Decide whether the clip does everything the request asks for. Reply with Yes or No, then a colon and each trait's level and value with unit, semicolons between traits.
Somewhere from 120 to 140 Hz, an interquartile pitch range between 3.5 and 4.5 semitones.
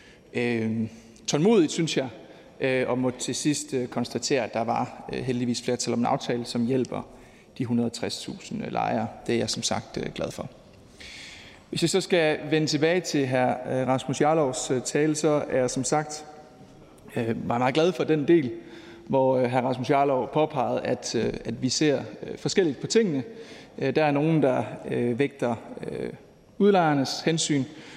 Yes: low, 135 Hz; average, 3.8 semitones